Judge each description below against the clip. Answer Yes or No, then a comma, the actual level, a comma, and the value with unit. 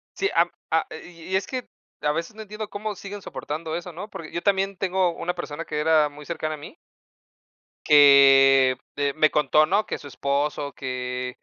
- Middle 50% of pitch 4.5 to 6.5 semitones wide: Yes, average, 4.9 semitones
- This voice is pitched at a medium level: Yes, medium, 155 Hz